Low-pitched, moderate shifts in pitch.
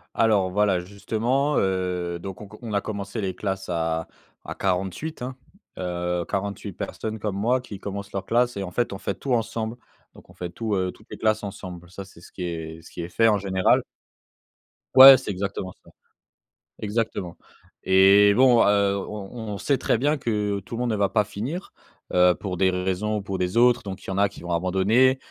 Yes: low, 100 Hz; average, 3.2 semitones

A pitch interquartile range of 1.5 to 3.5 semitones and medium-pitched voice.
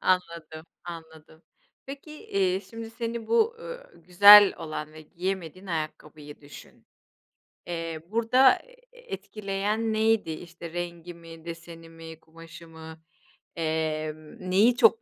No: average, 5.2 semitones; medium, 175 Hz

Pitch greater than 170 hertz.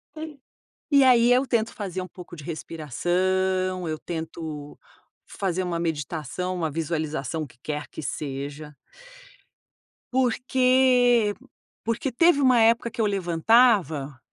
Yes: medium, 185 Hz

